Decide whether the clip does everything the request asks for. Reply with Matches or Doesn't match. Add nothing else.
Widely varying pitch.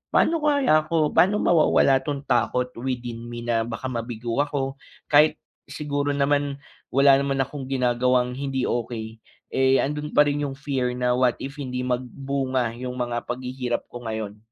Doesn't match